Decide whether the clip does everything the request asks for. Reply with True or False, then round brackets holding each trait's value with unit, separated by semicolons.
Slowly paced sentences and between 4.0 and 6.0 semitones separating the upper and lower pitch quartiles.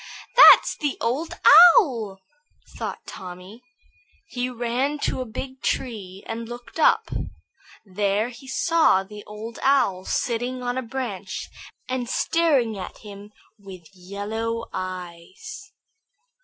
True (115 wpm; 4.7 semitones)